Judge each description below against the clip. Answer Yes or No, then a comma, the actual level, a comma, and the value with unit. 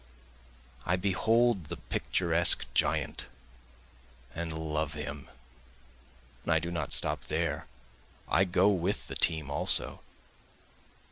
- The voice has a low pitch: Yes, very low, 85 Hz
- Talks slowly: Yes, slow, 110 wpm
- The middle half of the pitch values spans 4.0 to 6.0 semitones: No, average, 2.8 semitones